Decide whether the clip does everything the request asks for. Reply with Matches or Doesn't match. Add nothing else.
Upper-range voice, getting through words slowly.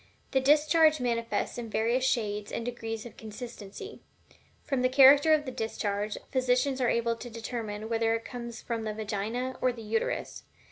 Doesn't match